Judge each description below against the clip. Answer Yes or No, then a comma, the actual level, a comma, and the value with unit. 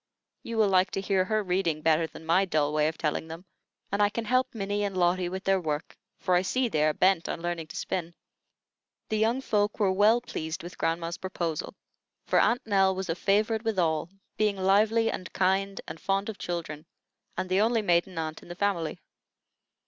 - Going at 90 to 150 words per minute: No, fast, 205 wpm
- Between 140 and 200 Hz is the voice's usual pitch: Yes, high, 190 Hz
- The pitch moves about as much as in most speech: Yes, average, 3.6 semitones